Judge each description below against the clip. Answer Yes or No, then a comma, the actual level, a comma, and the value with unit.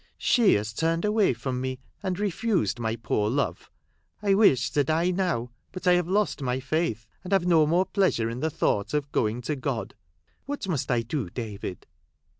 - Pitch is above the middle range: No, medium, 150 Hz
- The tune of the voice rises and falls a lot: Yes, wide, 7.4 semitones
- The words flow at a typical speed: Yes, average, 190 wpm